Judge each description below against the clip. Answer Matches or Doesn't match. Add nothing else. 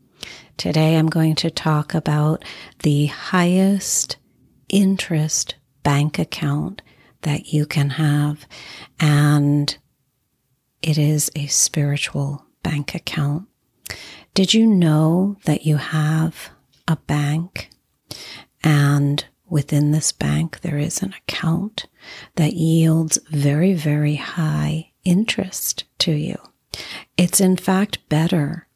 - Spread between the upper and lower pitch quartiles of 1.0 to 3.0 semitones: Matches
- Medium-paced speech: Doesn't match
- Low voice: Doesn't match